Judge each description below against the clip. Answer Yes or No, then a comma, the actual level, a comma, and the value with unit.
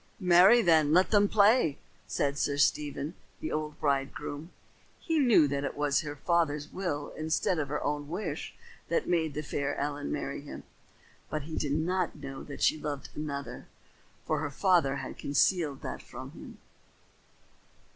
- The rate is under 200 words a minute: Yes, average, 160 wpm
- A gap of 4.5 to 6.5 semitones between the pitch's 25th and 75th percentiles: No, average, 3.2 semitones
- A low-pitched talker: No, medium, 150 Hz